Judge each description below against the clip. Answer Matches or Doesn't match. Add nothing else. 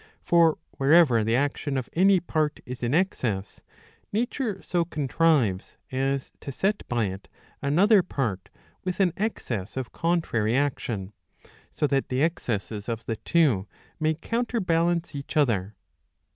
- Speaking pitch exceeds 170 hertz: Doesn't match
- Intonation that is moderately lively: Doesn't match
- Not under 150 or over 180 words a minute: Doesn't match